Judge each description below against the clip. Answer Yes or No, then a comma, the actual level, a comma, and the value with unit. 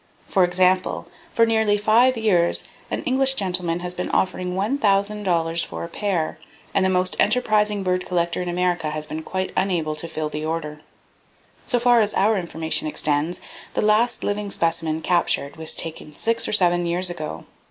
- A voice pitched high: No, medium, 180 Hz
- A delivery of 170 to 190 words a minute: Yes, average, 175 wpm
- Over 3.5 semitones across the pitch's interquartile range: Yes, average, 3.9 semitones